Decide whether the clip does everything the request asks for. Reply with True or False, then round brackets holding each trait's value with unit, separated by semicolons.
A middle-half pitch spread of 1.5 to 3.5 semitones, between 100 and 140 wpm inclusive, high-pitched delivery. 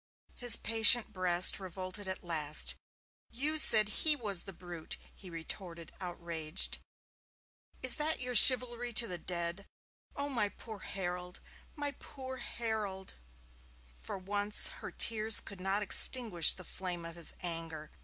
False (4.9 semitones; 135 wpm; 195 Hz)